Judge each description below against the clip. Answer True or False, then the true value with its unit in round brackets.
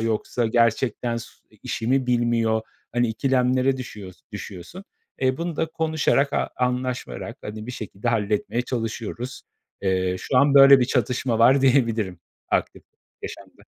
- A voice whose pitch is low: True (120 Hz)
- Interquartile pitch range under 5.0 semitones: True (2.9 semitones)